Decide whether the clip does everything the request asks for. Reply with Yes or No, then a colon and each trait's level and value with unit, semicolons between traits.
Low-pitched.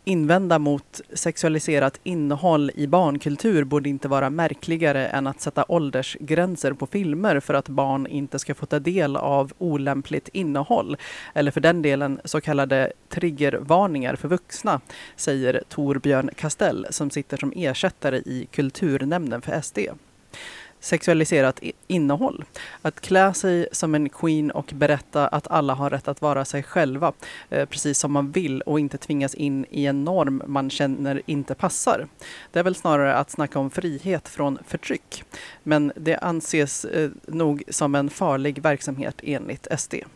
No: medium, 145 Hz